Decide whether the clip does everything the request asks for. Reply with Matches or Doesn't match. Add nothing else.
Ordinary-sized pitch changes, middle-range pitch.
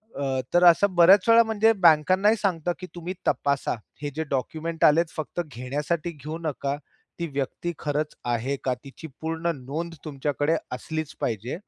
Matches